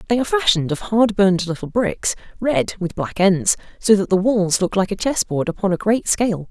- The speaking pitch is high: Yes, high, 200 Hz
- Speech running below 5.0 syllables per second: No, 5.5 syllables/s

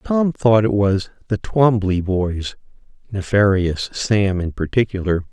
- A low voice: Yes, low, 100 Hz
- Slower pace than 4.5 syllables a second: Yes, 3.9 syllables/s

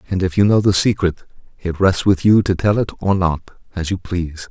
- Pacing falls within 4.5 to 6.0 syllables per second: Yes, 5.3 syllables/s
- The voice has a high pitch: No, very low, 90 Hz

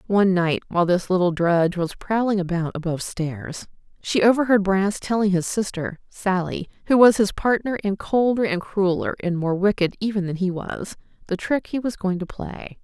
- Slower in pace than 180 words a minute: No, average, 185 wpm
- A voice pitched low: No, high, 190 Hz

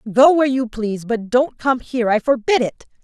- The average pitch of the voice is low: No, high, 245 Hz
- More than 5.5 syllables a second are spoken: Yes, 5.7 syllables/s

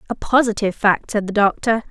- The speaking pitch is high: Yes, high, 215 Hz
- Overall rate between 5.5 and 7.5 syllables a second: Yes, 6.0 syllables/s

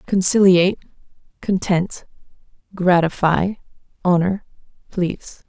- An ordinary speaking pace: No, slow, 55 wpm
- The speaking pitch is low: No, medium, 185 Hz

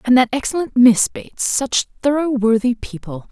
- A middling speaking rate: Yes, average, 145 wpm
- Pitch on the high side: Yes, high, 245 Hz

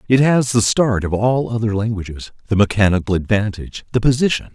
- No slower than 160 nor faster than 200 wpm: No, average, 145 wpm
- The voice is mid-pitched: No, low, 110 Hz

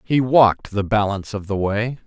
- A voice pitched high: No, low, 105 Hz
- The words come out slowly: No, fast, 205 wpm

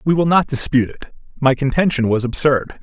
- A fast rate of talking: No, average, 190 wpm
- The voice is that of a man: Yes, male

